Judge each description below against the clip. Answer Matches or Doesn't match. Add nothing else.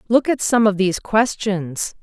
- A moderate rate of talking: Matches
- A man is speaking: Doesn't match